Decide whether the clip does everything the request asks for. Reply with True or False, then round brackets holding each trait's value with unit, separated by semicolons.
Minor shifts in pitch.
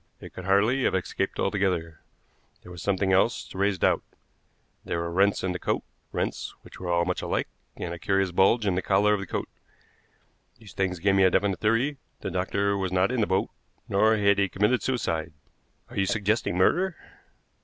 True (2.3 semitones)